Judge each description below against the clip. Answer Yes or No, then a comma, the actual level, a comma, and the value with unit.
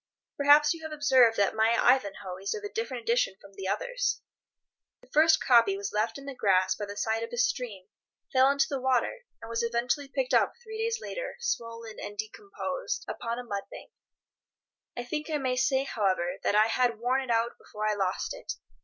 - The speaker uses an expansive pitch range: Yes, wide, 6.0 semitones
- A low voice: No, high, 245 Hz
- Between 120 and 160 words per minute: No, fast, 205 wpm